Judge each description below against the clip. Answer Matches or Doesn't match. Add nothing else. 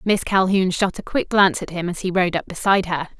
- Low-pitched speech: Doesn't match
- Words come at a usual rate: Doesn't match